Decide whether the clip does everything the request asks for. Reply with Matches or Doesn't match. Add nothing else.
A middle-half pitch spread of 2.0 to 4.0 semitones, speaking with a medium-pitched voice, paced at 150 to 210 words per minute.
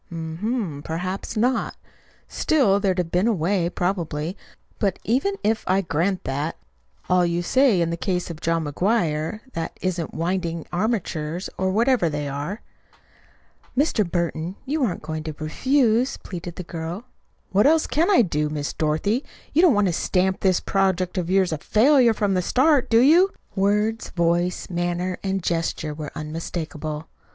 Doesn't match